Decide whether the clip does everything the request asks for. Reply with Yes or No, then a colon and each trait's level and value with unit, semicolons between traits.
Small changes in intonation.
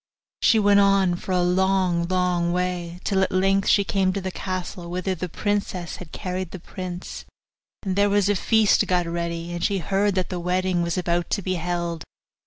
Yes: narrow, 1.8 semitones